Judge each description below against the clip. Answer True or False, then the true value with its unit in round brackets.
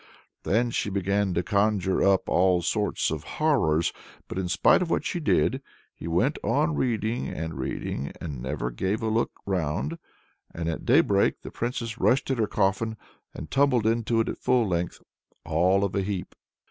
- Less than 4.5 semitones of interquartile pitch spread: False (5.1 semitones)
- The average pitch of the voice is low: True (100 Hz)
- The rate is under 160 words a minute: False (180 wpm)